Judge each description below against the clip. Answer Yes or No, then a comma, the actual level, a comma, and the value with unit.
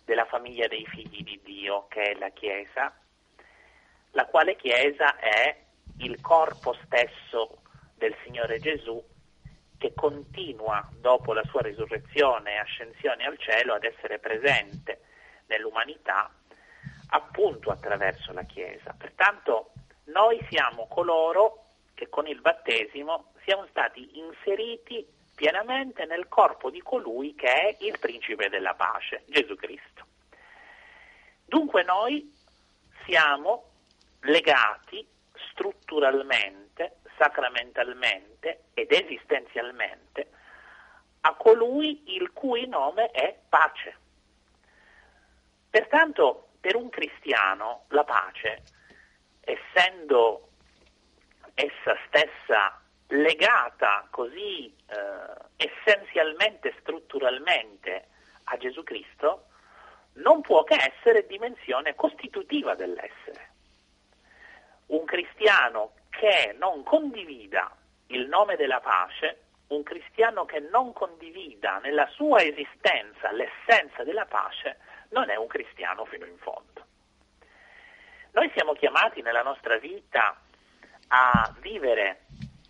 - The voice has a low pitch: No, high, 230 Hz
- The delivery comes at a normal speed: No, slow, 100 wpm